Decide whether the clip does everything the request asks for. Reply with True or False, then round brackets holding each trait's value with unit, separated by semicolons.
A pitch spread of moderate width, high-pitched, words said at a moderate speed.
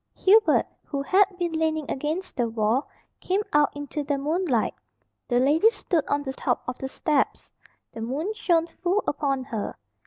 True (4.7 semitones; 295 Hz; 165 wpm)